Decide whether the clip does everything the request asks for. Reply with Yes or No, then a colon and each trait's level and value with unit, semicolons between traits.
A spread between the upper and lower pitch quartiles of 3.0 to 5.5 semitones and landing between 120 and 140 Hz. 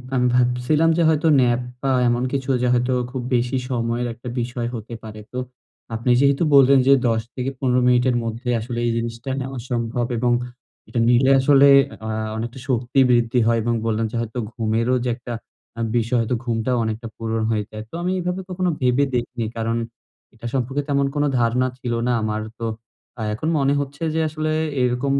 No: narrow, 2.5 semitones; low, 125 Hz